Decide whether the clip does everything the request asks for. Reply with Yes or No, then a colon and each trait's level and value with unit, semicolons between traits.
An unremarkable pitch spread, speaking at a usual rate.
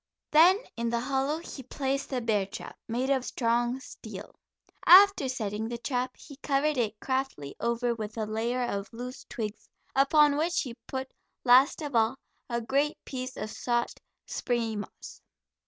Yes: average, 3.0 semitones; average, 160 wpm